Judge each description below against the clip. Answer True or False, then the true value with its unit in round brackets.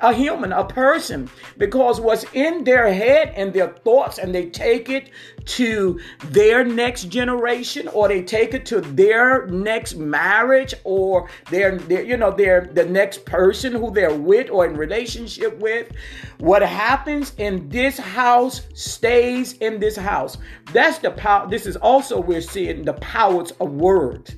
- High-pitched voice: True (230 Hz)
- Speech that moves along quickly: False (160 wpm)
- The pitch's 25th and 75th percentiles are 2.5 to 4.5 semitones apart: False (5.6 semitones)